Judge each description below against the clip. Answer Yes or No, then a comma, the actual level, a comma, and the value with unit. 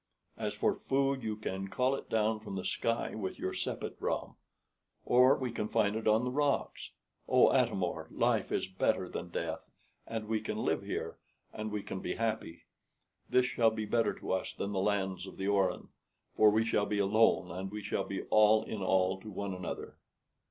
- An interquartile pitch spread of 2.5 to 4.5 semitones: Yes, average, 2.8 semitones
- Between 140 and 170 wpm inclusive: No, average, 200 wpm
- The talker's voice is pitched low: Yes, low, 105 Hz